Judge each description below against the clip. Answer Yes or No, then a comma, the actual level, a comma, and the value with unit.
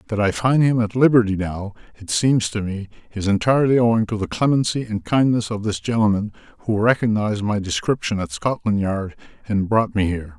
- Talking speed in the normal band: Yes, average, 190 wpm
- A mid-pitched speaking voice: No, low, 105 Hz